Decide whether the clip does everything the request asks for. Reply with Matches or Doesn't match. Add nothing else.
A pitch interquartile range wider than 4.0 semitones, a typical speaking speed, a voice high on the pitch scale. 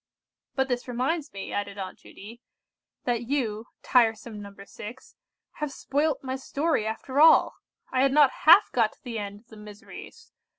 Matches